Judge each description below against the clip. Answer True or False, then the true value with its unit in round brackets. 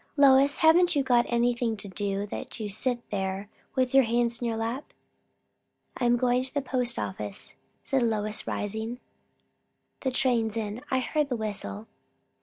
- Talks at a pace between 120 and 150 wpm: False (165 wpm)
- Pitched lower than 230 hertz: False (235 Hz)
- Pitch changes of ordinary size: True (3.4 semitones)